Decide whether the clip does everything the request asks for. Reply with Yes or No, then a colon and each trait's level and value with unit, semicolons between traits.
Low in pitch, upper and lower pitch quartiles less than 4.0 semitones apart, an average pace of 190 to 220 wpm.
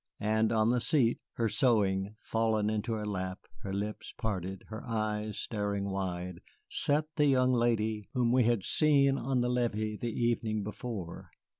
No: low, 110 Hz; average, 2.7 semitones; average, 160 wpm